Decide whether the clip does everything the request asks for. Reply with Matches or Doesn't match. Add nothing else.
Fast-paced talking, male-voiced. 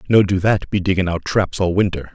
Matches